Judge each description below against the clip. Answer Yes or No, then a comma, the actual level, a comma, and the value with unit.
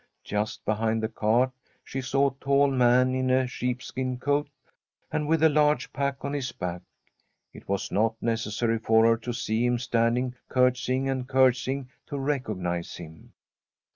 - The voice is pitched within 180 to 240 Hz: No, low, 125 Hz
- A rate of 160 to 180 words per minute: Yes, average, 165 wpm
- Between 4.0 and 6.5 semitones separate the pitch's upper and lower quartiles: No, average, 3.0 semitones